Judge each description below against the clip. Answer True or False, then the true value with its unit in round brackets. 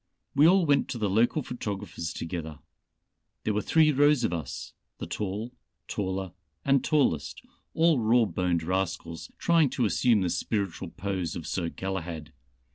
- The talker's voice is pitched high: False (100 Hz)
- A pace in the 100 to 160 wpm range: True (150 wpm)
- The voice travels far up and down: True (6.5 semitones)